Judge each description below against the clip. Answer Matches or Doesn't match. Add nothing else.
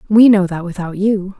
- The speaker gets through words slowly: Doesn't match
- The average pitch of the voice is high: Matches